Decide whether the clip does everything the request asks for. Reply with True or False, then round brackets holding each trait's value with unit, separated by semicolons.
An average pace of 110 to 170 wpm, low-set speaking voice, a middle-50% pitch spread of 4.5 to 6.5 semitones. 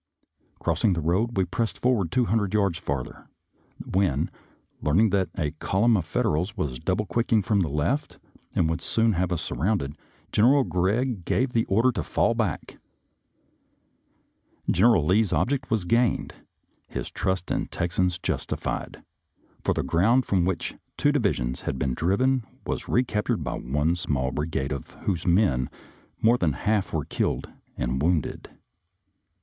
True (160 wpm; 95 Hz; 5.6 semitones)